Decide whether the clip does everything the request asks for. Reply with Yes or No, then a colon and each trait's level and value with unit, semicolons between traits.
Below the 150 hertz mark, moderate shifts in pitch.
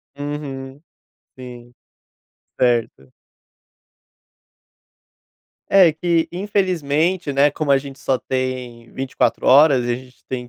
Yes: low, 135 Hz; average, 3.5 semitones